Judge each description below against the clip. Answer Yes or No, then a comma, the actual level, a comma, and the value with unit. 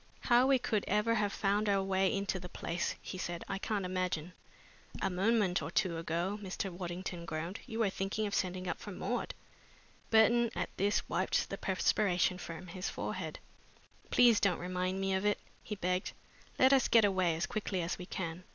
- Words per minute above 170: Yes, average, 190 wpm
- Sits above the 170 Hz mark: Yes, high, 190 Hz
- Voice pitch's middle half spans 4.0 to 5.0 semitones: No, narrow, 2.5 semitones